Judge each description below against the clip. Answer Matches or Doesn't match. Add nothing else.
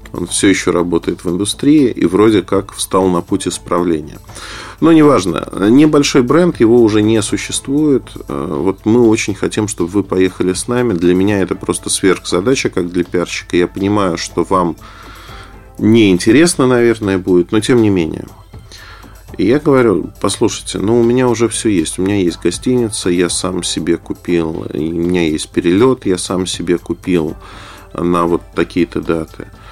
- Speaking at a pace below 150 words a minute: Doesn't match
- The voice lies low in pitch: Matches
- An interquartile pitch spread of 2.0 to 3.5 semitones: Doesn't match